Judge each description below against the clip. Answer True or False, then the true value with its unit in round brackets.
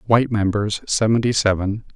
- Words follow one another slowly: True (125 wpm)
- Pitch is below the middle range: True (105 Hz)